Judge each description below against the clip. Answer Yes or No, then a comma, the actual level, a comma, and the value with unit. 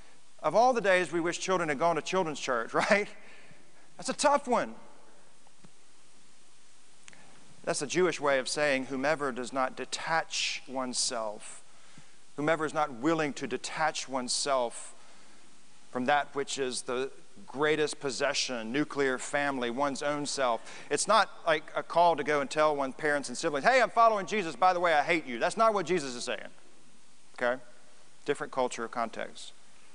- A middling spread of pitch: Yes, average, 4.7 semitones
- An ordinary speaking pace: Yes, average, 160 wpm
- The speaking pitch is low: No, medium, 150 Hz